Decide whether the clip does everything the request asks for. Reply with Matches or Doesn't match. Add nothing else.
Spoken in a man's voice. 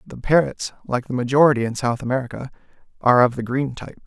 Matches